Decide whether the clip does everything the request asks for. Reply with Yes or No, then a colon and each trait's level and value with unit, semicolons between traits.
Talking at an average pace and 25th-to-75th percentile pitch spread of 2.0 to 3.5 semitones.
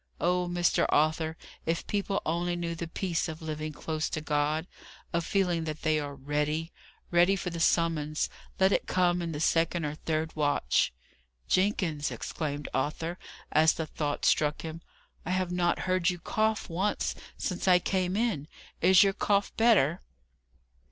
Yes: average, 160 wpm; average, 2.7 semitones